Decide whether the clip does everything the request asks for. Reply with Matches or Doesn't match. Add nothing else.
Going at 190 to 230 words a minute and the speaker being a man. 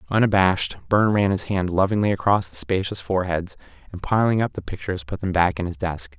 Matches